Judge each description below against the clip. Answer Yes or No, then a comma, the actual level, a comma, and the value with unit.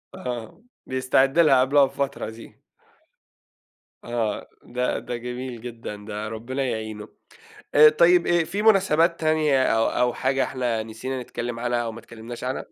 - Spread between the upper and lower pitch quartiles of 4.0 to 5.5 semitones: No, average, 3.6 semitones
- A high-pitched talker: No, low, 125 Hz